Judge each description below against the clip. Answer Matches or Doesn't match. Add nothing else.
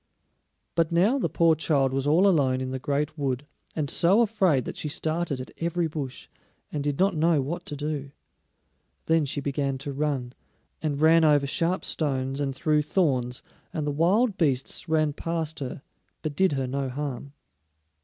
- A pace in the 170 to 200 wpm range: Matches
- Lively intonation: Doesn't match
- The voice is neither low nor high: Matches